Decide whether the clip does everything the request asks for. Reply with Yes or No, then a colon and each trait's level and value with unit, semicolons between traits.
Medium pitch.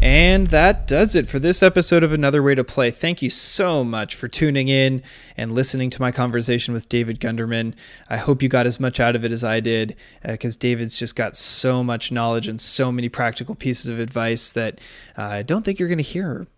No: low, 125 Hz